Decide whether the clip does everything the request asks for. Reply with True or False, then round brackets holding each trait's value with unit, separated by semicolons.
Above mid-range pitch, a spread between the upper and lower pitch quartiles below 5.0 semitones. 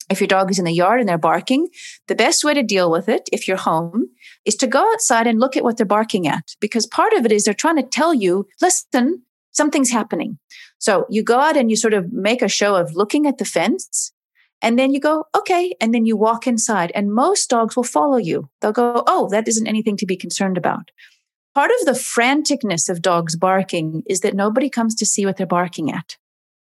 False (225 Hz; 5.6 semitones)